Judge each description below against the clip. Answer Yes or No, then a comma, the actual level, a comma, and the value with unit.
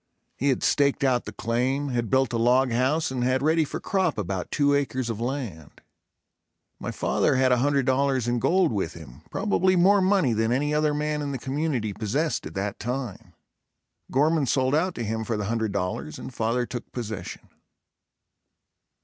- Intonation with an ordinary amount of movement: Yes, average, 4.2 semitones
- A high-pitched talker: No, low, 130 Hz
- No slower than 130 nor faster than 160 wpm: No, average, 175 wpm